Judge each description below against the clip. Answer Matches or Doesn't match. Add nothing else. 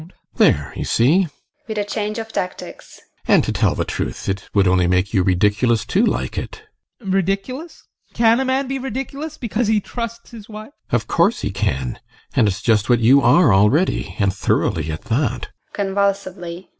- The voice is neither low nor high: Matches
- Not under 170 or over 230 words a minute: Matches